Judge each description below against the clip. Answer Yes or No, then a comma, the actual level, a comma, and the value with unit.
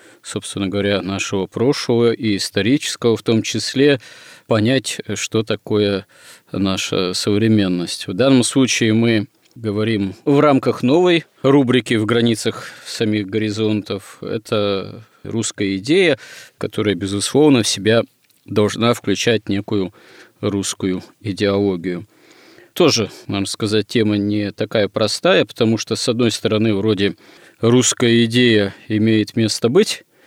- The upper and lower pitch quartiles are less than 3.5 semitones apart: Yes, narrow, 2.5 semitones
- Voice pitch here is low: Yes, low, 110 Hz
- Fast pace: No, average, 115 wpm